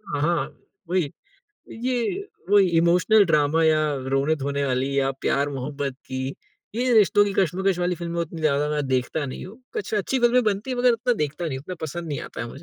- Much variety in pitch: Yes, wide, 6.3 semitones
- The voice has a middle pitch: Yes, medium, 165 Hz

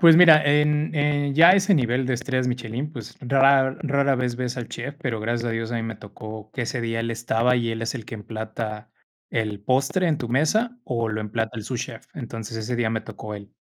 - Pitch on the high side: No, low, 120 Hz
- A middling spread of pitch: Yes, average, 3.8 semitones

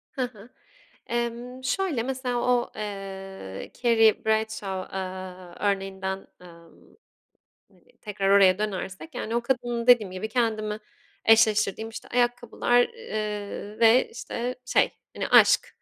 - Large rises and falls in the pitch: No, average, 3.7 semitones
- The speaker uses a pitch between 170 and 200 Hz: No, high, 220 Hz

